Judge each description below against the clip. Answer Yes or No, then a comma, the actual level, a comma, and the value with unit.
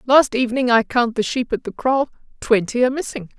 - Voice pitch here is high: Yes, high, 240 Hz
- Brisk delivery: No, average, 195 wpm